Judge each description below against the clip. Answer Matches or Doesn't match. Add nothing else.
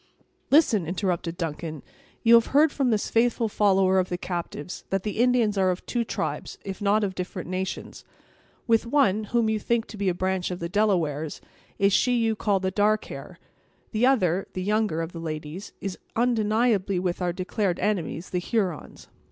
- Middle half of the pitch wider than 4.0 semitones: Doesn't match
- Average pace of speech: Matches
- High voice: Matches